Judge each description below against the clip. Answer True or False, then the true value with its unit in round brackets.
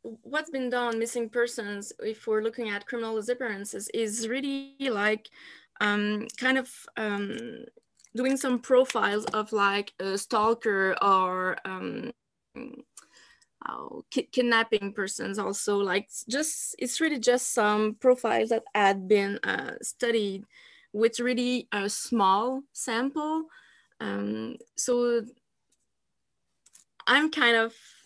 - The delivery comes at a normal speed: False (115 wpm)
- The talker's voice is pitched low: False (230 Hz)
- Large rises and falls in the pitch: False (3.3 semitones)